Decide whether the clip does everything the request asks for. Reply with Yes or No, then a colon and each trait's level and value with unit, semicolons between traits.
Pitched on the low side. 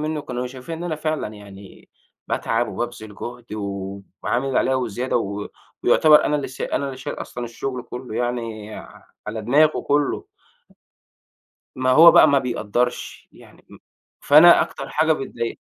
Yes: low, 125 Hz